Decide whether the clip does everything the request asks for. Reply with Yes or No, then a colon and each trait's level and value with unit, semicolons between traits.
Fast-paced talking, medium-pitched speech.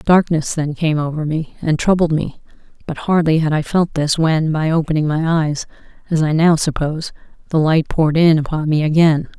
No: average, 190 wpm; medium, 160 Hz